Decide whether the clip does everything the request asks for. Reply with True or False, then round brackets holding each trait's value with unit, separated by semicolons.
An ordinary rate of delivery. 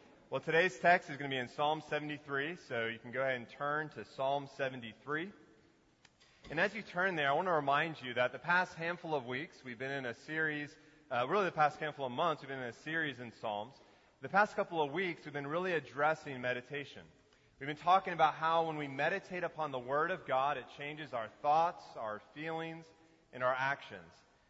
False (215 wpm)